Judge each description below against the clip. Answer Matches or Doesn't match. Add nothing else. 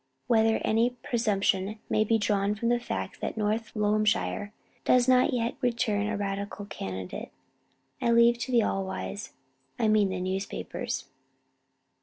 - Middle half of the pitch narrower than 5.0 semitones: Matches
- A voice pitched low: Doesn't match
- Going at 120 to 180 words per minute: Matches